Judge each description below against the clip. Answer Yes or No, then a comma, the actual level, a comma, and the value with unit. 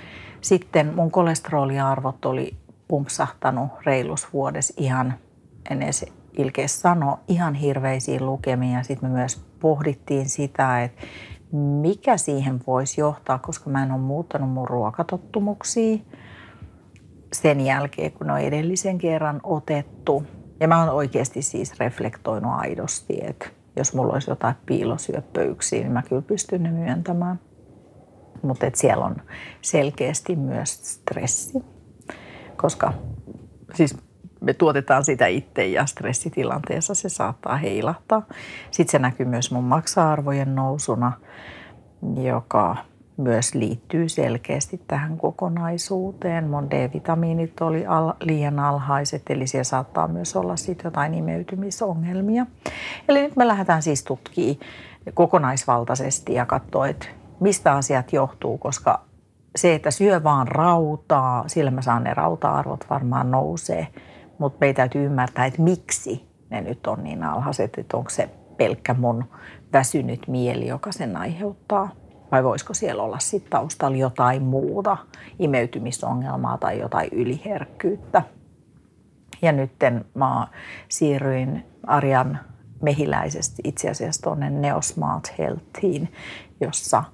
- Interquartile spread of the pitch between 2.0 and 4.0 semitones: No, average, 4.8 semitones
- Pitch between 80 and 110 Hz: No, medium, 140 Hz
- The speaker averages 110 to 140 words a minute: Yes, average, 120 wpm